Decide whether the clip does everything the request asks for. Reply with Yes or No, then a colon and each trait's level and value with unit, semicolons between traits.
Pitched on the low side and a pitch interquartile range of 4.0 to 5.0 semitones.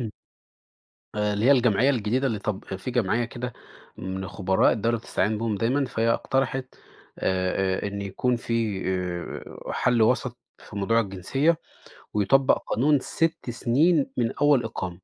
Yes: low, 115 Hz; average, 4.4 semitones